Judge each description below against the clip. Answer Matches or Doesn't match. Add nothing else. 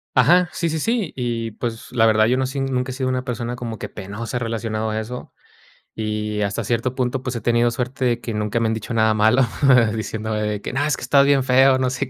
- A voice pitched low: Matches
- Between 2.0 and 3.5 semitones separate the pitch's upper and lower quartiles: Matches